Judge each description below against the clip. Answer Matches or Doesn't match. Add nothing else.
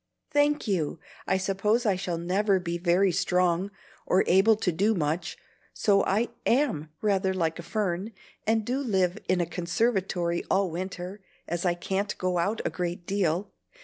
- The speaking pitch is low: Doesn't match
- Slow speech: Doesn't match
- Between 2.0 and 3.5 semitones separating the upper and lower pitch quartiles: Matches